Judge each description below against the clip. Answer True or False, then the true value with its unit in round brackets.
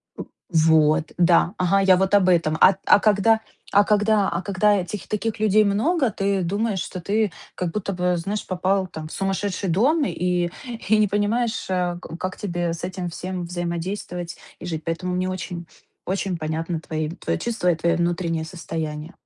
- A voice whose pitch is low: False (185 Hz)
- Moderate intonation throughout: True (3.0 semitones)